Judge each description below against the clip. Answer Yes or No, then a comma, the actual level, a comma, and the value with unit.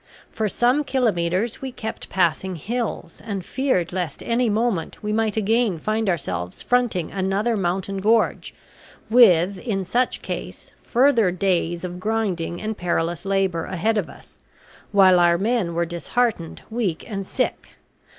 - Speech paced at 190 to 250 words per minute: No, average, 145 wpm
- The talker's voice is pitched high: Yes, high, 195 Hz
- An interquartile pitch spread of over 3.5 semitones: Yes, average, 4.3 semitones